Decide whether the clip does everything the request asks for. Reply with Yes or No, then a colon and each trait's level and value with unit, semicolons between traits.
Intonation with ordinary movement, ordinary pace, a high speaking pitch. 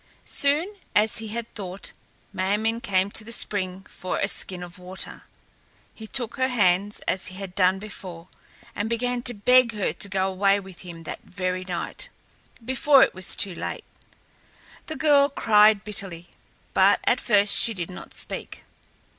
Yes: average, 3.8 semitones; average, 170 wpm; high, 200 Hz